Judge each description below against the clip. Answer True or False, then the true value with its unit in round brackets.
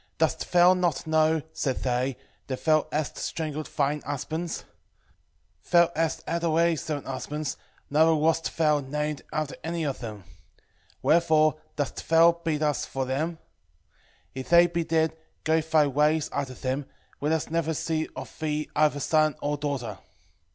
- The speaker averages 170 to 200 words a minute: False (155 wpm)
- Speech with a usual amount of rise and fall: False (2.1 semitones)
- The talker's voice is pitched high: False (155 Hz)